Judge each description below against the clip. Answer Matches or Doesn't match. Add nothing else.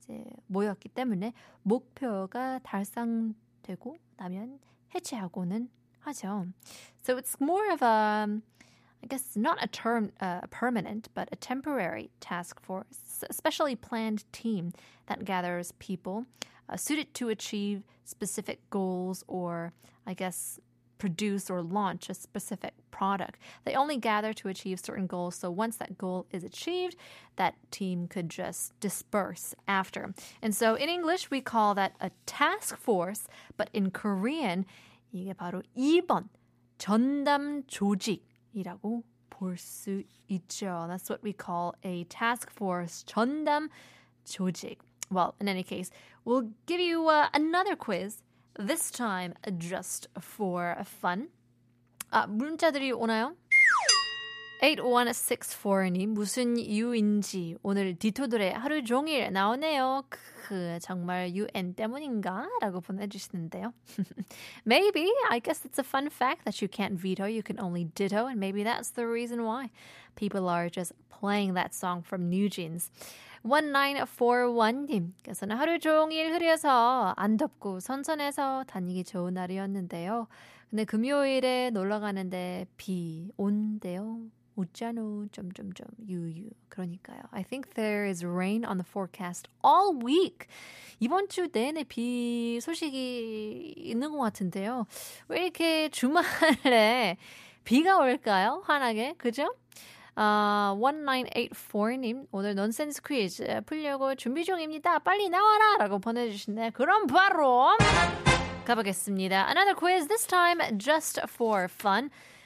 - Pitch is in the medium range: Doesn't match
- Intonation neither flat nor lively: Doesn't match